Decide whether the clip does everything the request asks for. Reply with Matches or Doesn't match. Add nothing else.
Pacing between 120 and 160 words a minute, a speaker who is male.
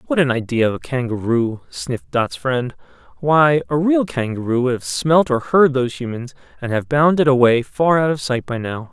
Doesn't match